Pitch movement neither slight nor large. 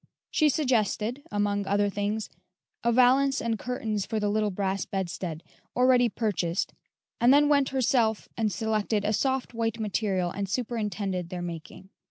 Yes: average, 3.6 semitones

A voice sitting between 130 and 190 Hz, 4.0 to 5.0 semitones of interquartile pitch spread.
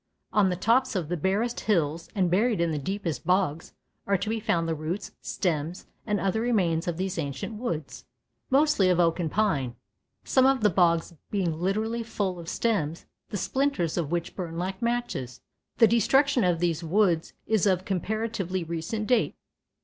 Yes: medium, 185 Hz; average, 4.6 semitones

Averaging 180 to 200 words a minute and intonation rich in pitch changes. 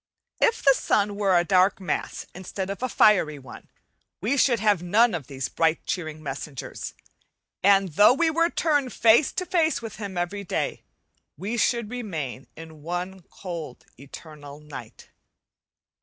No: average, 155 wpm; wide, 6.4 semitones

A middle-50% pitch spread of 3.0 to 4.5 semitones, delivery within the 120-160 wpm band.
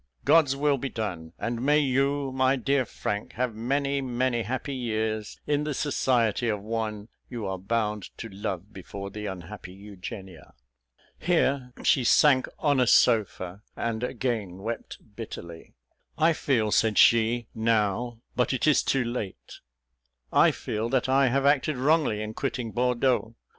Yes: average, 3.9 semitones; average, 150 wpm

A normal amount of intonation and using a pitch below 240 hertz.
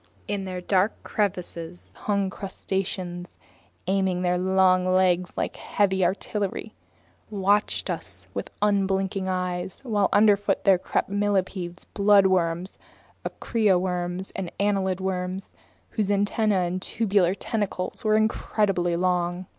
No: narrow, 2.0 semitones; high, 190 Hz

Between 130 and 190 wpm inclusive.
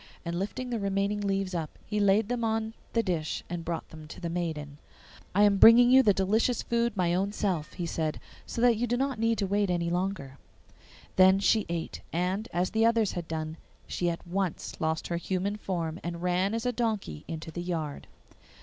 No: average, 200 wpm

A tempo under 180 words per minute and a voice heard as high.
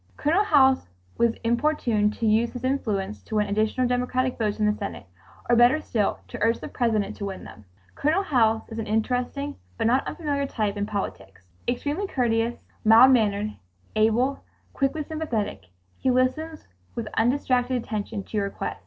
Yes: average, 165 wpm; high, 235 Hz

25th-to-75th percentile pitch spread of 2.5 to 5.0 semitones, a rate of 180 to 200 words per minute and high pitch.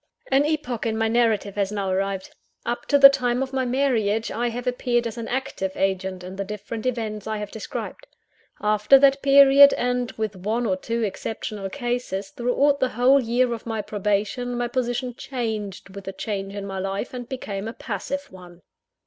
Yes: average, 3.8 semitones; average, 190 wpm; high, 230 Hz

